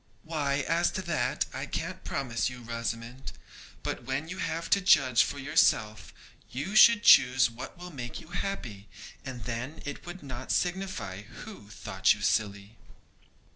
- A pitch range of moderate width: No, wide, 6.5 semitones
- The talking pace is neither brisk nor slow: Yes, average, 155 wpm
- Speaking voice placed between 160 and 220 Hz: No, low, 130 Hz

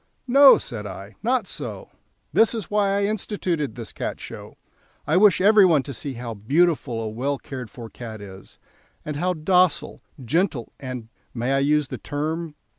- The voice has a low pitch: No, medium, 150 Hz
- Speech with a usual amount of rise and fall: No, wide, 7.4 semitones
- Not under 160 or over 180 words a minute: Yes, average, 175 wpm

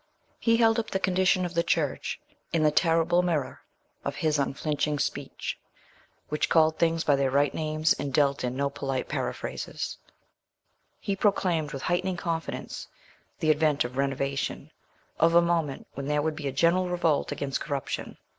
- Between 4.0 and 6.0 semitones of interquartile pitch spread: No, average, 3.5 semitones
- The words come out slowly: No, average, 160 wpm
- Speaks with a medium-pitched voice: Yes, medium, 155 Hz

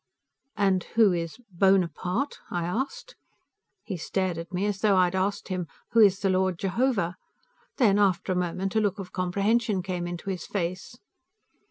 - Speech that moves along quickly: No, average, 170 wpm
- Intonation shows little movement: Yes, narrow, 2.3 semitones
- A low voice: No, high, 190 Hz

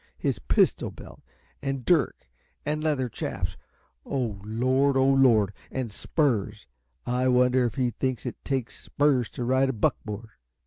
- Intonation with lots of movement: No, average, 2.7 semitones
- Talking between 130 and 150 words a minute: Yes, average, 145 wpm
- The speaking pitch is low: Yes, low, 130 Hz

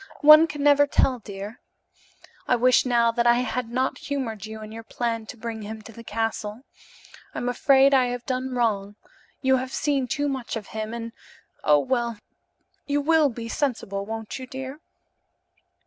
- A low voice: No, high, 240 Hz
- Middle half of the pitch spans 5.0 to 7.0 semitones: No, average, 3.0 semitones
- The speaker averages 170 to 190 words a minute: Yes, average, 175 wpm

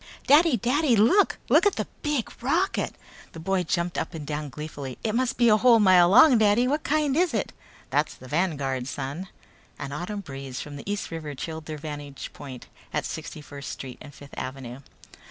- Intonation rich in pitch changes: Yes, wide, 8.8 semitones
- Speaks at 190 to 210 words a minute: Yes, average, 195 wpm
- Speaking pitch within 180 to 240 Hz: No, medium, 170 Hz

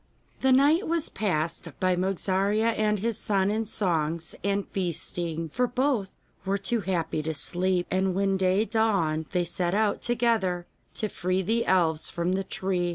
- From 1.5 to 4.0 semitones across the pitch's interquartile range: Yes, average, 3.6 semitones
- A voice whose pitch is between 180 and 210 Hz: Yes, high, 190 Hz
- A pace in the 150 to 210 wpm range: Yes, average, 160 wpm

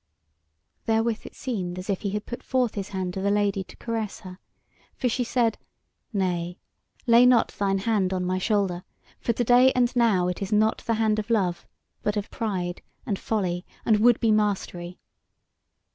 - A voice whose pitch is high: Yes, high, 210 Hz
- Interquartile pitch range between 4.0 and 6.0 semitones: No, average, 3.6 semitones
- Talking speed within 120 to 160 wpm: No, average, 185 wpm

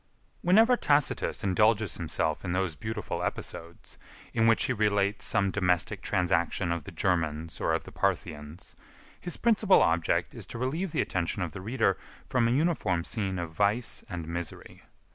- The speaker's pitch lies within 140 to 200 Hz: No, low, 100 Hz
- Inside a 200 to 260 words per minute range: No, average, 160 wpm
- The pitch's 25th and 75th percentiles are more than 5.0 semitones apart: Yes, wide, 5.4 semitones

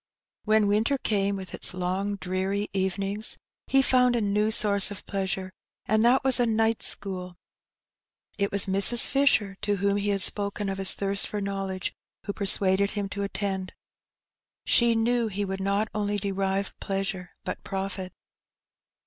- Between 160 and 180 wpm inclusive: Yes, average, 165 wpm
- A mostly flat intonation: Yes, narrow, 1.7 semitones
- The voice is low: No, high, 200 Hz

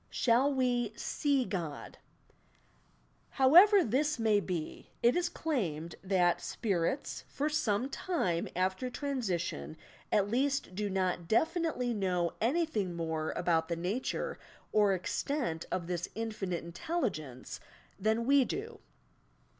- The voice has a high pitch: Yes, high, 215 Hz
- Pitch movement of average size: No, wide, 7.5 semitones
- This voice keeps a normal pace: No, slow, 115 wpm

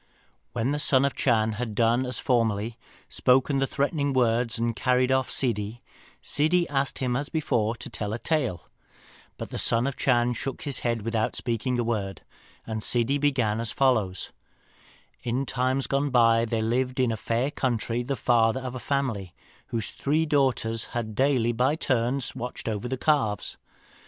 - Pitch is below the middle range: Yes, low, 120 Hz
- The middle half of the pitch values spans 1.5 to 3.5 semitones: Yes, average, 2.9 semitones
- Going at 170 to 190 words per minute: Yes, average, 180 wpm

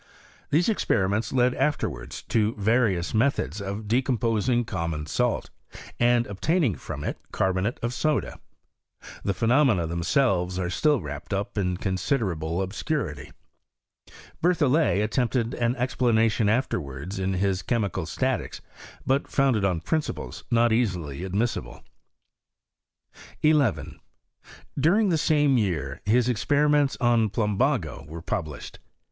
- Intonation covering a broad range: Yes, wide, 5.8 semitones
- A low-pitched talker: Yes, low, 110 Hz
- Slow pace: Yes, slow, 115 wpm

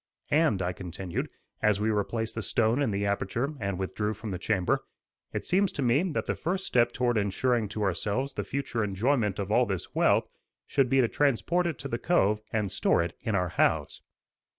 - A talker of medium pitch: No, low, 110 Hz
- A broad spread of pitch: No, average, 4.8 semitones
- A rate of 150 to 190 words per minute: No, average, 200 wpm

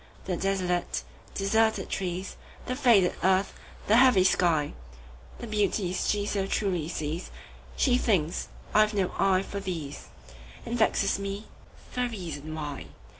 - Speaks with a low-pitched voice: No, high, 190 Hz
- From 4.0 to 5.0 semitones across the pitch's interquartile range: Yes, average, 4.3 semitones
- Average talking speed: No, slow, 120 wpm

